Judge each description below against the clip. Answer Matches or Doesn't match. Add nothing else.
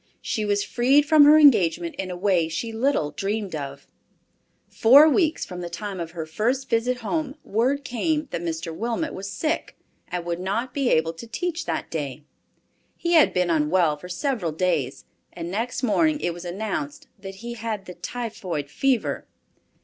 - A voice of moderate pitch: Doesn't match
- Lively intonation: Matches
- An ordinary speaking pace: Matches